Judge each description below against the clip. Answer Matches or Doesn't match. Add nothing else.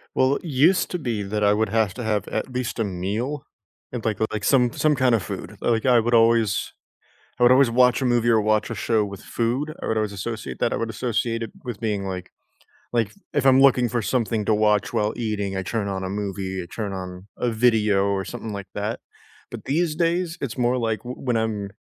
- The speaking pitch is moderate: Doesn't match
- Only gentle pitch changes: Doesn't match